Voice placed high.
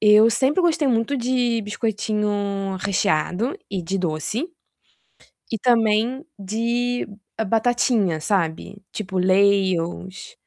Yes: high, 210 Hz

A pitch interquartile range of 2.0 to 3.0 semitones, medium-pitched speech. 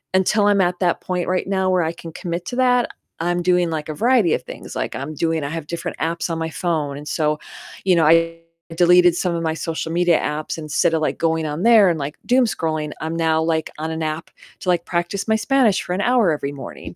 Yes: narrow, 2.5 semitones; medium, 165 Hz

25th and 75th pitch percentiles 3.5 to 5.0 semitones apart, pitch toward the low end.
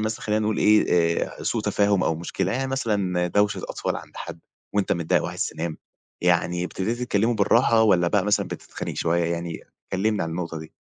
Yes: average, 3.8 semitones; very low, 95 Hz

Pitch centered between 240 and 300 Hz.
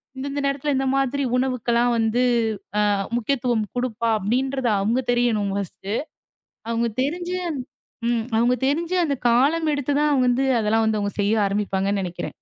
Yes: high, 245 Hz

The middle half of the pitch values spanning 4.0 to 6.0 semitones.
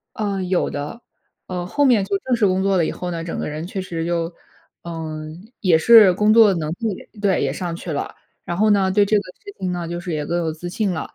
No: average, 3.5 semitones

